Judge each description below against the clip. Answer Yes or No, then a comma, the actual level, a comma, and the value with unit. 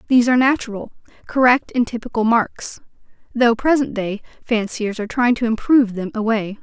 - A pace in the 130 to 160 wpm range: Yes, average, 155 wpm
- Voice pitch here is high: Yes, high, 235 Hz